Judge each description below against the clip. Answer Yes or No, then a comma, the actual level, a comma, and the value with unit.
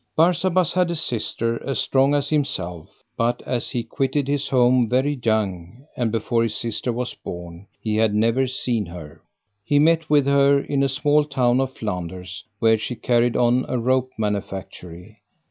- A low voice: Yes, low, 120 Hz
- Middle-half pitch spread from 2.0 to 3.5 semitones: No, average, 4.6 semitones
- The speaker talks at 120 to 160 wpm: No, average, 170 wpm